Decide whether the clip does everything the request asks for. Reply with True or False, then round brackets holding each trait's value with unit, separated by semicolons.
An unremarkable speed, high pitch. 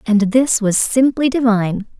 True (150 wpm; 230 Hz)